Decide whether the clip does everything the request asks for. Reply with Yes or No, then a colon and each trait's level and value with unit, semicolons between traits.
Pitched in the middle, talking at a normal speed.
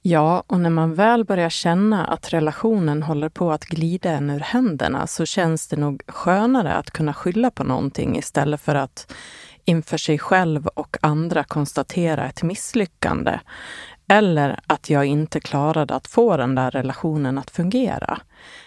Yes: medium, 160 Hz; average, 155 wpm